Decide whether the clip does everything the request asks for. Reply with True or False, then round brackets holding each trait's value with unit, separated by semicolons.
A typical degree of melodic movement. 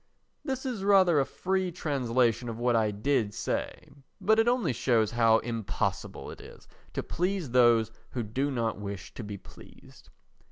False (8.1 semitones)